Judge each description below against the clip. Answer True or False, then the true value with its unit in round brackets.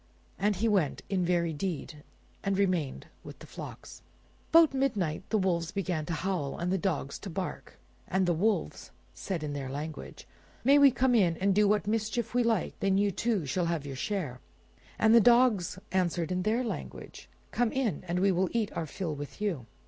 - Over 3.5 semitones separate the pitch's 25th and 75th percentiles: True (4.3 semitones)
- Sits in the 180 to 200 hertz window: True (190 Hz)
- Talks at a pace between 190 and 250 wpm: True (195 wpm)